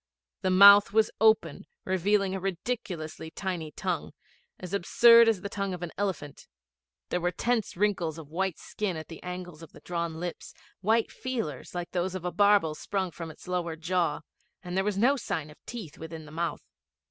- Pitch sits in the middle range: Yes, medium, 180 Hz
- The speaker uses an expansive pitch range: No, average, 3.5 semitones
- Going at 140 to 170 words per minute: No, average, 185 wpm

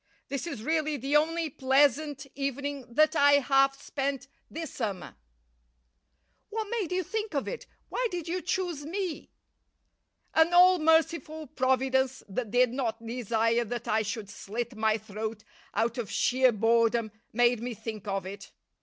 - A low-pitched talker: No, very high, 265 Hz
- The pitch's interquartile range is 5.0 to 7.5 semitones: Yes, wide, 5.4 semitones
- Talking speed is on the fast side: No, average, 150 wpm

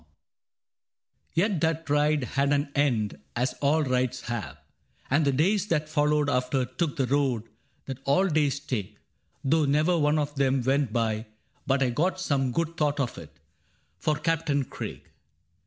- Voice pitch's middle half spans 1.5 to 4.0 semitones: Yes, average, 3.1 semitones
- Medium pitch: Yes, medium, 145 Hz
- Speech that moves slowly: No, average, 165 wpm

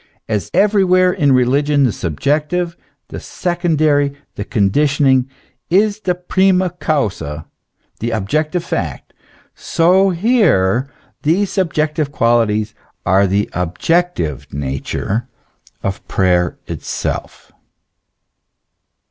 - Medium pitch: Yes, medium, 145 Hz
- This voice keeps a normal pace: No, slow, 90 wpm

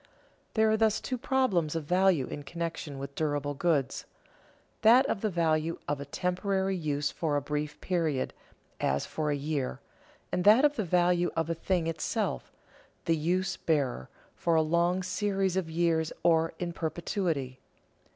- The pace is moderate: Yes, average, 160 wpm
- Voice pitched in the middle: Yes, medium, 165 Hz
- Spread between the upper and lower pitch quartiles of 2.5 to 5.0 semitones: Yes, average, 3.8 semitones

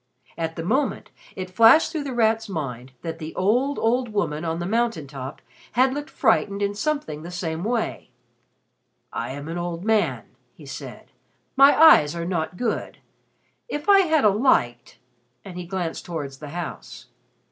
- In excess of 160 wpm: Yes, average, 170 wpm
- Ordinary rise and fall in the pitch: No, wide, 6.8 semitones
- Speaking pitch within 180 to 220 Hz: Yes, medium, 185 Hz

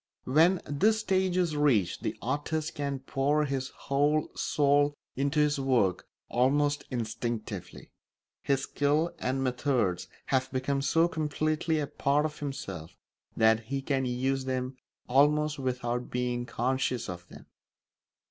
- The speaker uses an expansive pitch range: No, average, 2.9 semitones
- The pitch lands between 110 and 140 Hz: Yes, low, 135 Hz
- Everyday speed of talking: No, slow, 130 wpm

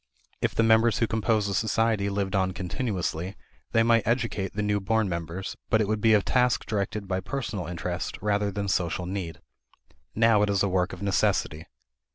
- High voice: No, low, 100 Hz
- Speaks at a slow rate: No, average, 190 wpm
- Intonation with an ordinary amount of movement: Yes, average, 3.0 semitones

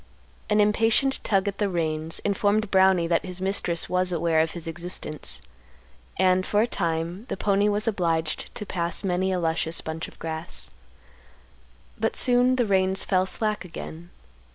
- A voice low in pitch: No, medium, 185 Hz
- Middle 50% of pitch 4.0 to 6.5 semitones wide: No, average, 3.6 semitones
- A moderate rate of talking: Yes, average, 160 wpm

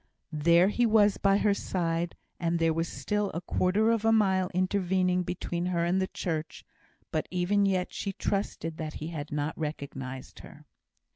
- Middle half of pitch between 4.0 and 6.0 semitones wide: No, average, 3.1 semitones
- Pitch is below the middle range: No, medium, 180 Hz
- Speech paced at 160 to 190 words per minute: Yes, average, 165 wpm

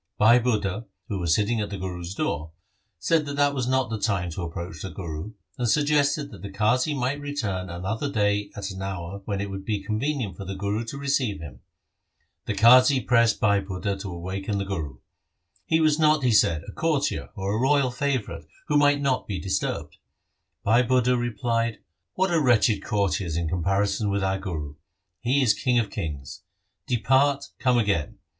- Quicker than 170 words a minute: Yes, average, 185 wpm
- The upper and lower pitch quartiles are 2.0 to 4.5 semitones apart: No, average, 5.1 semitones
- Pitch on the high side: No, low, 105 Hz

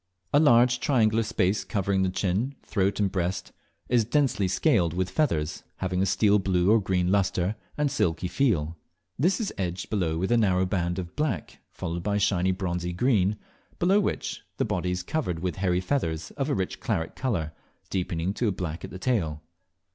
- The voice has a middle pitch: No, very low, 95 Hz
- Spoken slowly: No, average, 185 wpm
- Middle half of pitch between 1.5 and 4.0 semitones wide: No, average, 4.4 semitones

